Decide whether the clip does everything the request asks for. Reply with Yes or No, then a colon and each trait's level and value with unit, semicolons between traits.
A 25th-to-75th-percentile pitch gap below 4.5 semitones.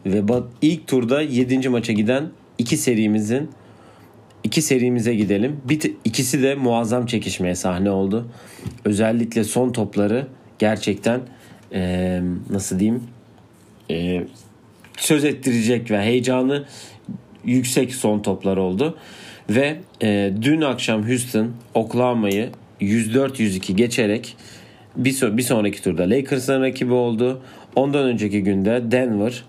Yes: average, 3.5 semitones